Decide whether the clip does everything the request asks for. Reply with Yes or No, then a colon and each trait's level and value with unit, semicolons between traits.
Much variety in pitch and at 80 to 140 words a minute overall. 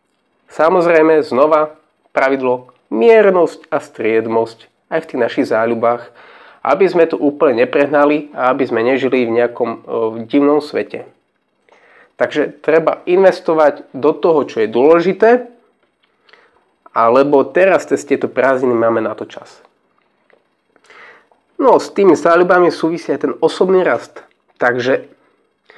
Yes: wide, 5.7 semitones; average, 125 wpm